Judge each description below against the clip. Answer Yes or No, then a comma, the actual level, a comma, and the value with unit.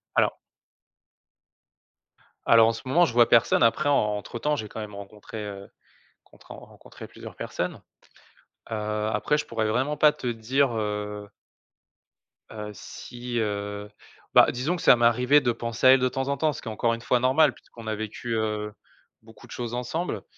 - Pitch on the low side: Yes, low, 115 Hz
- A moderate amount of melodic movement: Yes, average, 3.2 semitones